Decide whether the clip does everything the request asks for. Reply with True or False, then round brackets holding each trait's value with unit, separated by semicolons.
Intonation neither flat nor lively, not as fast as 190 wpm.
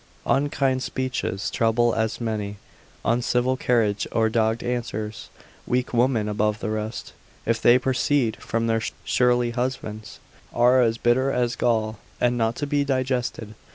False (2.3 semitones; 140 wpm)